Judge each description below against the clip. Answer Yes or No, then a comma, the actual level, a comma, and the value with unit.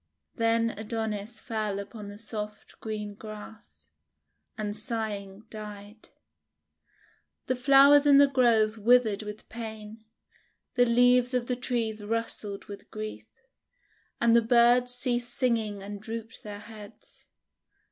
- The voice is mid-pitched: No, high, 220 Hz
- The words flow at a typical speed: No, slow, 120 wpm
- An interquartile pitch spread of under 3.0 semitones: Yes, narrow, 2.4 semitones